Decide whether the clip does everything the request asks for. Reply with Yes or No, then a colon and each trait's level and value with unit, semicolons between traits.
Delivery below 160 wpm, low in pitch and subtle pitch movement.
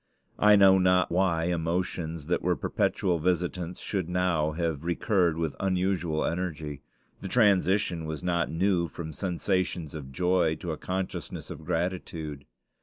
Yes: average, 140 wpm; very low, 85 Hz; narrow, 2.3 semitones